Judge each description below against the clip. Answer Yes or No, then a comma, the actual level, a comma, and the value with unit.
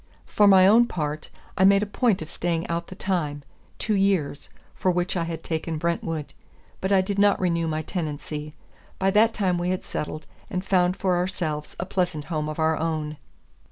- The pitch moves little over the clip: No, average, 3.5 semitones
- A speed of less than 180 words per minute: No, average, 190 wpm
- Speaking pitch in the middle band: Yes, medium, 175 Hz